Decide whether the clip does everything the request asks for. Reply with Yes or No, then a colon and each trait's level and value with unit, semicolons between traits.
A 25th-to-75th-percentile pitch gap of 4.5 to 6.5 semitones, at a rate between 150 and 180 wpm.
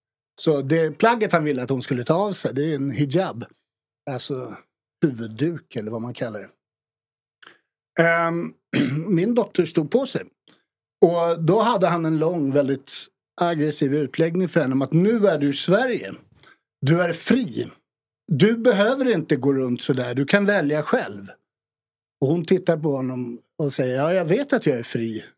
Yes: average, 4.8 semitones; average, 175 wpm